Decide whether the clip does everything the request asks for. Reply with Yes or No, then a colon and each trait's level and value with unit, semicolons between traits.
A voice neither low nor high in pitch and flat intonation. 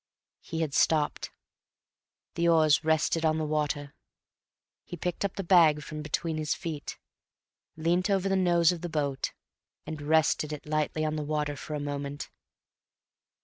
Yes: medium, 155 Hz; narrow, 2.0 semitones